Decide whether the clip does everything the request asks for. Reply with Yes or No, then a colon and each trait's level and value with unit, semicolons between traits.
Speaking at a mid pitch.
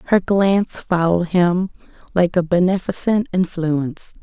Yes: medium, 180 Hz